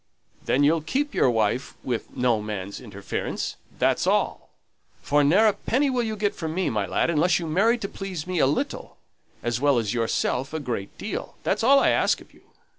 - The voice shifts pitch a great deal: Yes, wide, 8.7 semitones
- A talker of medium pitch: Yes, medium, 150 Hz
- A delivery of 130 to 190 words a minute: No, average, 200 wpm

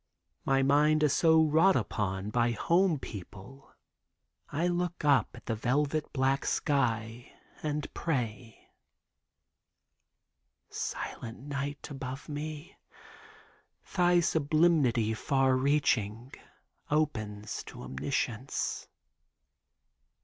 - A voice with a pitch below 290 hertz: Yes, medium, 140 Hz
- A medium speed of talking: No, slow, 85 wpm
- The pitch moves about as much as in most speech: Yes, average, 4.7 semitones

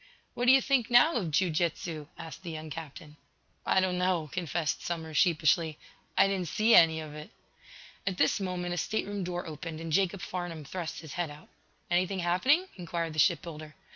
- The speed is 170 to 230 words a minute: Yes, average, 190 wpm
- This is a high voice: No, medium, 175 Hz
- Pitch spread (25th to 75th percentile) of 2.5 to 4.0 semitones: Yes, average, 2.8 semitones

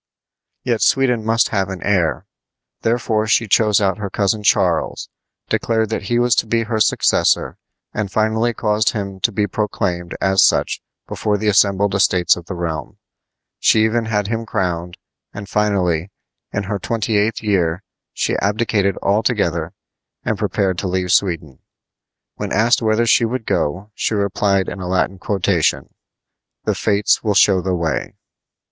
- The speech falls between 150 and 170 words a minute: Yes, average, 155 wpm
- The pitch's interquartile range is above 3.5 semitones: No, average, 2.8 semitones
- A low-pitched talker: Yes, low, 100 Hz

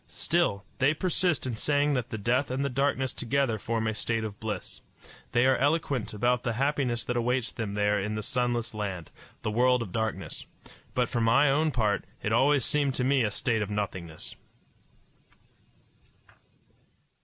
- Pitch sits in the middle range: No, low, 120 Hz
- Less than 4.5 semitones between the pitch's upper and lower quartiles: Yes, average, 4.0 semitones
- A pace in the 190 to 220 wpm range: No, average, 170 wpm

